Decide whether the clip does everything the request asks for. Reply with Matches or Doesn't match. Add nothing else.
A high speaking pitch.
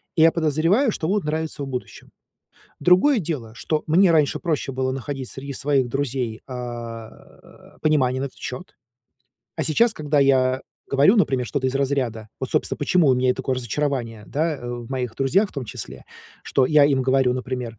Doesn't match